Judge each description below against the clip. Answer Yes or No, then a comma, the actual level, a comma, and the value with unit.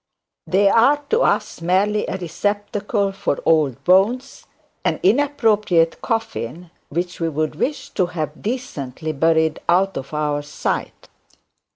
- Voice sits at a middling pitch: Yes, medium, 180 Hz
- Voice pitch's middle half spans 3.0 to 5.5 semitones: Yes, average, 4.8 semitones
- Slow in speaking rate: Yes, slow, 130 wpm